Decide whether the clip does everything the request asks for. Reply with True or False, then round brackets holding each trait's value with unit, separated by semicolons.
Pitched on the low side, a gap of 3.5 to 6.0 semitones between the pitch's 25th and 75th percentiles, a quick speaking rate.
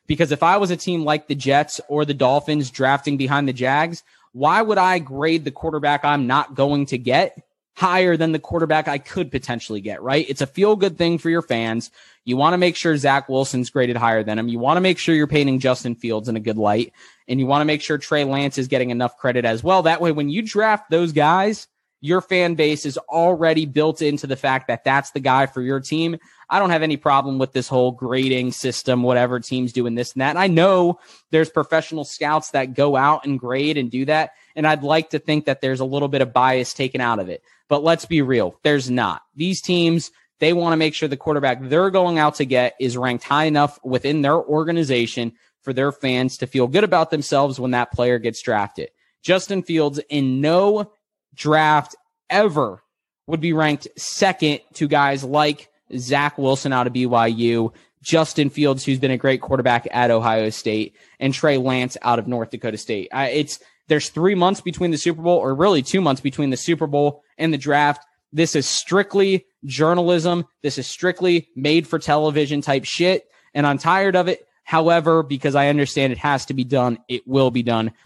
False (145 Hz; 3.9 semitones; 215 wpm)